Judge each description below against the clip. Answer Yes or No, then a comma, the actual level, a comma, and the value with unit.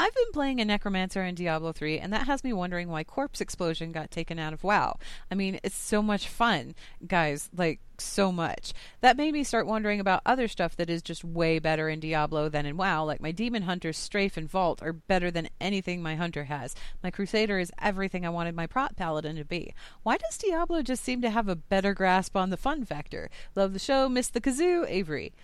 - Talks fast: Yes, fast, 225 wpm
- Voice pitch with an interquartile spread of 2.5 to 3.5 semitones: No, average, 5.2 semitones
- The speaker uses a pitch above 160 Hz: Yes, medium, 185 Hz